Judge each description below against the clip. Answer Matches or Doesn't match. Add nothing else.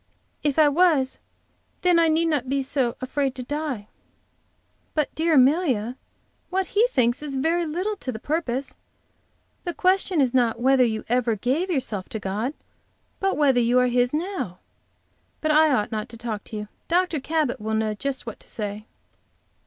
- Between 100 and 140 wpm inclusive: Doesn't match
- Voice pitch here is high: Matches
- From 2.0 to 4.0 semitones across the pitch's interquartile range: Doesn't match